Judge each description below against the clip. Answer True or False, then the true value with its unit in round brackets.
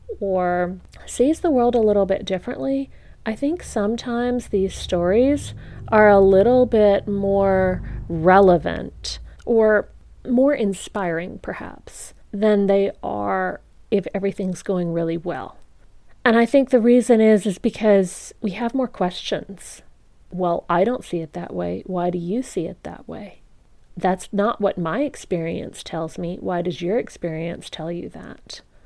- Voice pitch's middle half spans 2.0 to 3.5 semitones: False (4.7 semitones)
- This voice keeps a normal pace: True (150 wpm)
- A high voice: True (195 Hz)